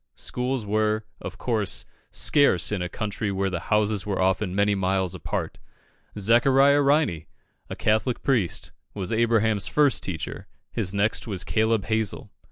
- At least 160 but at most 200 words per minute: No, average, 145 wpm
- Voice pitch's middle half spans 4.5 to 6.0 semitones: No, average, 3.2 semitones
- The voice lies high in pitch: No, low, 105 Hz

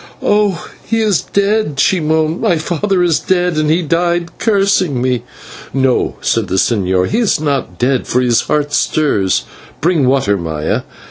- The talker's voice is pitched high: No, medium, 155 Hz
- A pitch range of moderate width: No, wide, 6.2 semitones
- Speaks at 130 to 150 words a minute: No, average, 160 wpm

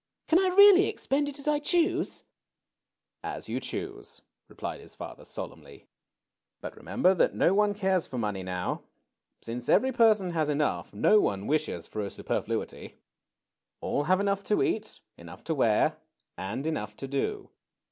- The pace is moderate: Yes, average, 160 wpm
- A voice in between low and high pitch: Yes, medium, 175 Hz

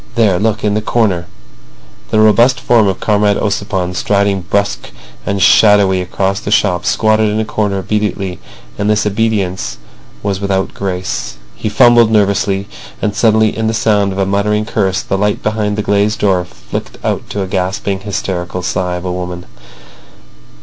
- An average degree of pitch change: No, narrow, 2.0 semitones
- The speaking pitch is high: No, low, 100 Hz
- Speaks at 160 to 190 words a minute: Yes, average, 165 wpm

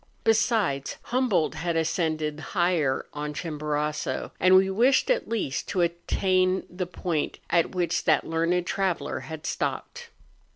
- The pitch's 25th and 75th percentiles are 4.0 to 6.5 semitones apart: No, average, 3.5 semitones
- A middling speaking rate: No, slow, 130 wpm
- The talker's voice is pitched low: No, medium, 175 Hz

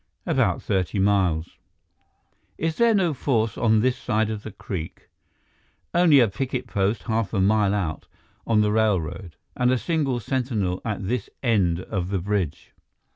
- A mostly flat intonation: No, average, 4.5 semitones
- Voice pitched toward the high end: No, low, 110 Hz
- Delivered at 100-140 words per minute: No, average, 155 wpm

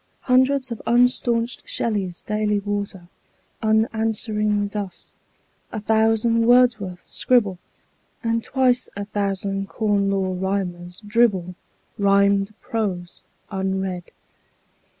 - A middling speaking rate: No, slow, 90 wpm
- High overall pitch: Yes, high, 205 Hz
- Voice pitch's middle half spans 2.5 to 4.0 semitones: Yes, average, 2.8 semitones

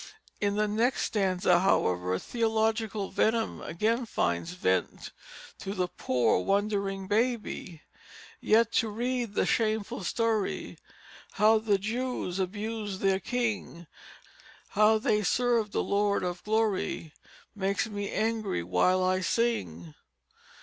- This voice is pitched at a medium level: No, high, 205 Hz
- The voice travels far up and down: No, average, 3.2 semitones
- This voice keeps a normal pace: No, slow, 115 wpm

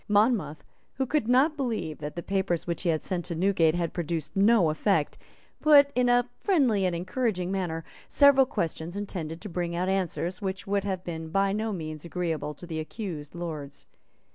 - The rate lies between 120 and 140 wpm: No, average, 185 wpm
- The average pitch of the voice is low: No, medium, 185 Hz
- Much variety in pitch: No, average, 4.7 semitones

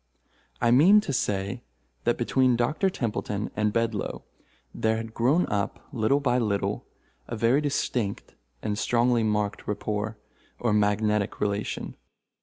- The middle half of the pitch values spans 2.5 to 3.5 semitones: Yes, average, 2.9 semitones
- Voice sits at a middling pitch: No, low, 115 Hz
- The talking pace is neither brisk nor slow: No, slow, 130 wpm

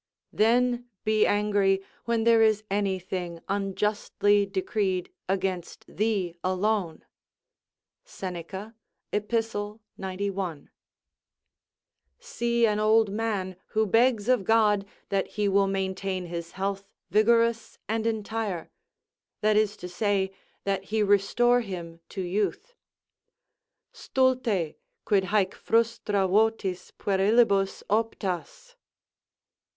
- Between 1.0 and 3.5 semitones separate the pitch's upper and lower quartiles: Yes, average, 2.7 semitones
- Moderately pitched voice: No, high, 205 Hz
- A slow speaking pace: Yes, slow, 100 wpm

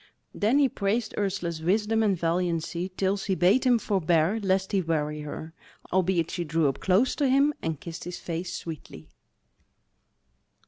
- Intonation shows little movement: No, average, 4.0 semitones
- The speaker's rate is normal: Yes, average, 155 wpm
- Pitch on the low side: No, medium, 185 Hz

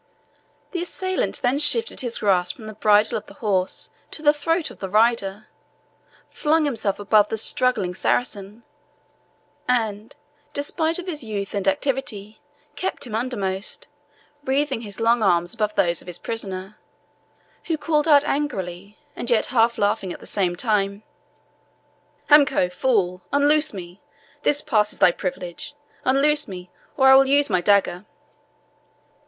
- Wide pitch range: Yes, wide, 6.3 semitones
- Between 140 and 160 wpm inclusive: Yes, average, 145 wpm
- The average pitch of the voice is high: Yes, high, 220 Hz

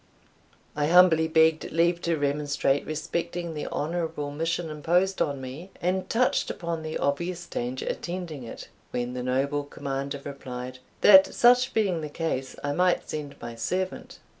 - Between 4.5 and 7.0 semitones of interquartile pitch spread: No, average, 3.6 semitones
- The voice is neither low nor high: Yes, medium, 155 Hz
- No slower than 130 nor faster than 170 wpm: Yes, average, 150 wpm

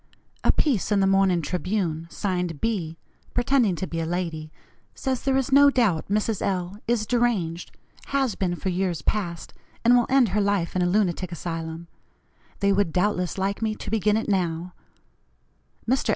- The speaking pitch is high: Yes, high, 195 Hz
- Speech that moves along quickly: No, average, 170 wpm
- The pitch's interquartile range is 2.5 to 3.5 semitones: No, average, 4.2 semitones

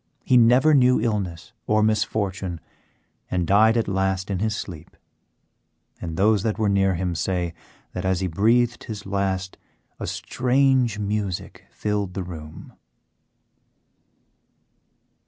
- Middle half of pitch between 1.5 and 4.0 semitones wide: Yes, average, 3.0 semitones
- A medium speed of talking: No, slow, 125 wpm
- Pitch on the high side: No, low, 100 Hz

